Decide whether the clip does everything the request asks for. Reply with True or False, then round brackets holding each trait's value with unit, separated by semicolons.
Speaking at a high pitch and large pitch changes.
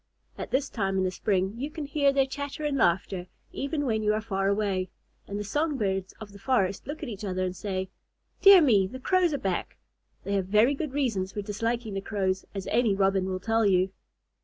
True (210 Hz; 5.7 semitones)